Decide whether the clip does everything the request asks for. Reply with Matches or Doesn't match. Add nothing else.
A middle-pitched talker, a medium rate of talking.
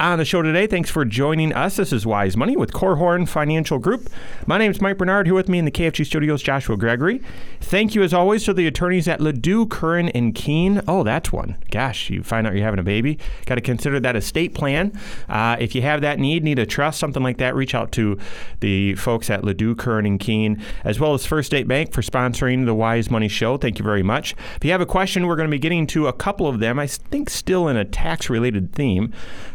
Doesn't match